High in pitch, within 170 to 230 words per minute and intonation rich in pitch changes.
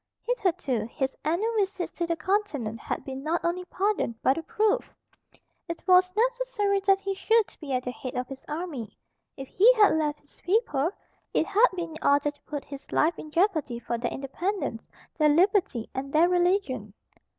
Yes: very high, 335 Hz; average, 180 wpm; wide, 6.4 semitones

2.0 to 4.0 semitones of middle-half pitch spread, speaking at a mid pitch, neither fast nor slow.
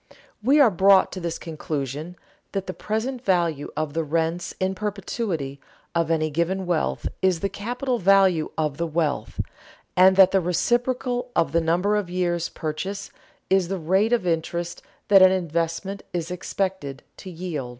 Yes: average, 3.3 semitones; medium, 180 Hz; average, 160 wpm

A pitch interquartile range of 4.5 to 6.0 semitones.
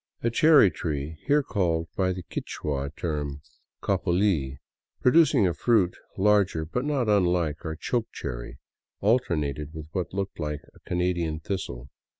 Yes: average, 5.3 semitones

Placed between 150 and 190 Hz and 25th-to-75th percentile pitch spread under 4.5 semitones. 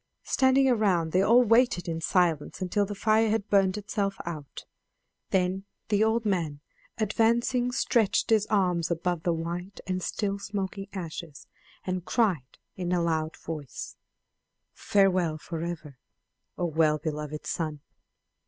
Yes: medium, 185 Hz; average, 4.1 semitones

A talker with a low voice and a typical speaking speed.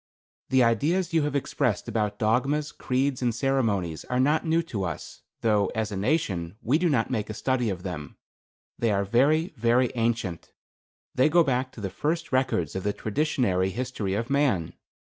Yes: low, 120 Hz; average, 180 wpm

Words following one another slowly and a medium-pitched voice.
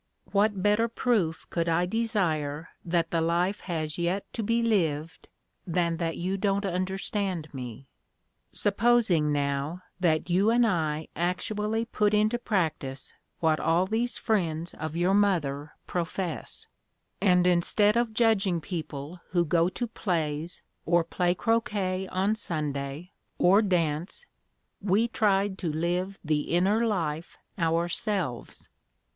Yes: slow, 130 wpm; medium, 180 Hz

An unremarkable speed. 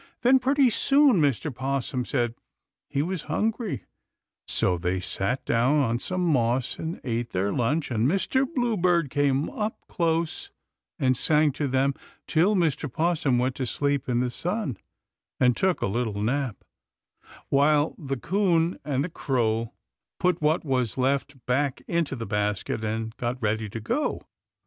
Yes: average, 155 wpm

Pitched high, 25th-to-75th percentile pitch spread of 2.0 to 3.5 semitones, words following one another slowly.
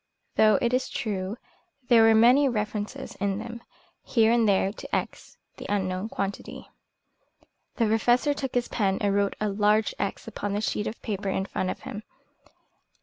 No: high, 215 Hz; average, 2.8 semitones; average, 170 wpm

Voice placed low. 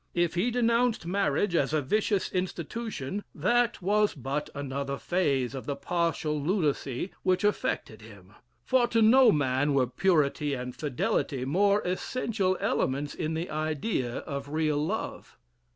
No: medium, 155 Hz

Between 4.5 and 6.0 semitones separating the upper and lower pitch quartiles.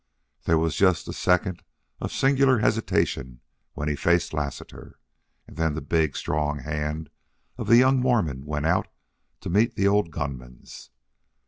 Yes: average, 5.2 semitones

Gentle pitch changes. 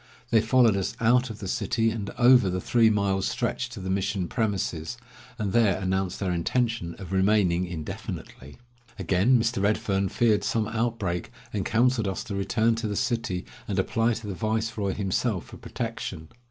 No: average, 3.3 semitones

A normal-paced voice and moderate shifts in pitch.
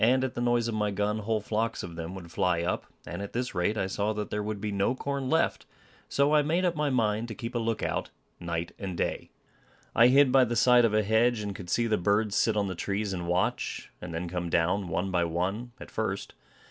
No: fast, 245 wpm; average, 4.5 semitones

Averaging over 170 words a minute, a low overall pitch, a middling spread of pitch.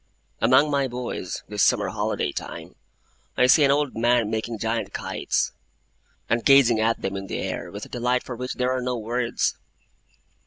No: average, 180 wpm; low, 120 Hz; narrow, 2.1 semitones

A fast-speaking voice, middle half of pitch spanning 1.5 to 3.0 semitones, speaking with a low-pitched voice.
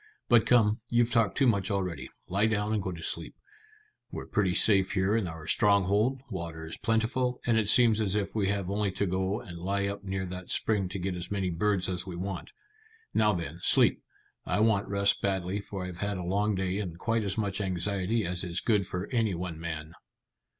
Yes: fast, 210 wpm; narrow, 2.6 semitones; low, 100 Hz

